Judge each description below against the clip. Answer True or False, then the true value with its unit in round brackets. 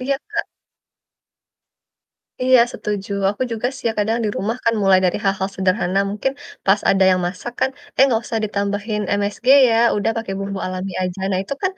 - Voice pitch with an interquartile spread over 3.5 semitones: False (2.9 semitones)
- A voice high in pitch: True (205 Hz)